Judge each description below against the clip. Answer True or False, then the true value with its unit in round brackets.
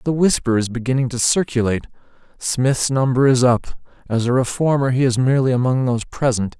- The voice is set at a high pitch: False (125 Hz)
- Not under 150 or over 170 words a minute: True (165 wpm)